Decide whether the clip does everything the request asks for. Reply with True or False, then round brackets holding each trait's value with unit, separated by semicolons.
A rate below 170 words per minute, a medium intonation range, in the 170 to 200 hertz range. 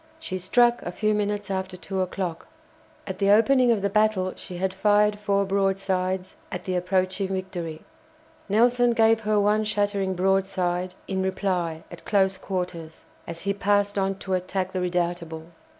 False (160 wpm; 1.9 semitones; 190 Hz)